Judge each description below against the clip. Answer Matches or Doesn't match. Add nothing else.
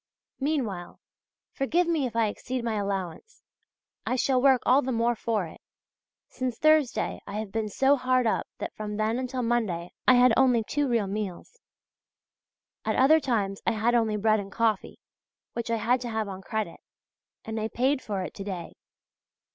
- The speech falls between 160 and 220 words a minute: Matches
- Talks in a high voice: Matches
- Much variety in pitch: Doesn't match